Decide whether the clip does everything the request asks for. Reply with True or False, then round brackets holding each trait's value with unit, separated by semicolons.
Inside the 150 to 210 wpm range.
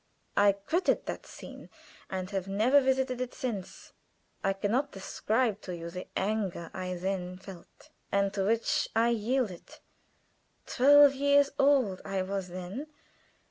False (140 wpm)